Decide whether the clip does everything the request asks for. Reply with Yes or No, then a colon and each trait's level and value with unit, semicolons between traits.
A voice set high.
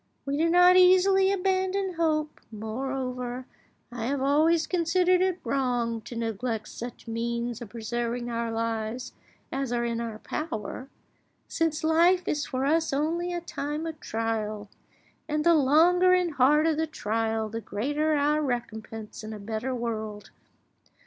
Yes: very high, 265 Hz